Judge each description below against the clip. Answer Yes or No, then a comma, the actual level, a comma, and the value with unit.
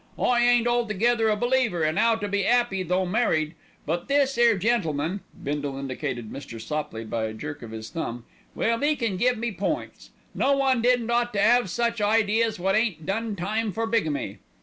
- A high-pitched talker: Yes, high, 210 Hz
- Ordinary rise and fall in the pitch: No, wide, 7.1 semitones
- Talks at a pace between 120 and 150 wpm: No, average, 190 wpm